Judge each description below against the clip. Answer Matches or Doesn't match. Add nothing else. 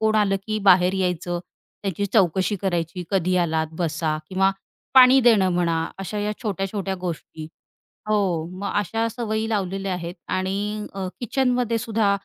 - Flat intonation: Doesn't match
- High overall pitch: Matches